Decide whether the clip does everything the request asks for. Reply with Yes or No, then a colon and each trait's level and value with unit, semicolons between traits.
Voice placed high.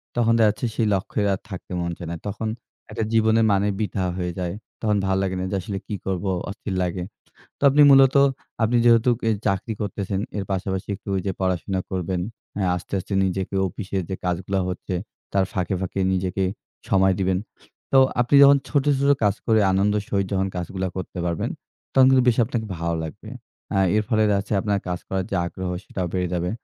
No: very low, 95 Hz